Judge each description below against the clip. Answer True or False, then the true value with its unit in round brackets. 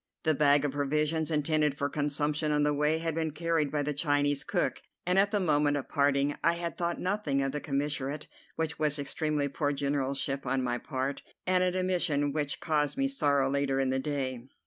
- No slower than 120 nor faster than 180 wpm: False (200 wpm)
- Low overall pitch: False (145 Hz)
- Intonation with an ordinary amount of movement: False (2.2 semitones)